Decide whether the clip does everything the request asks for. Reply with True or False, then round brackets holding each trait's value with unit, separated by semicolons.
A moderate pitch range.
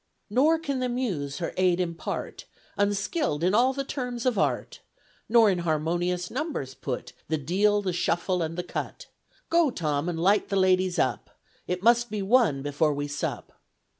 False (6.4 semitones)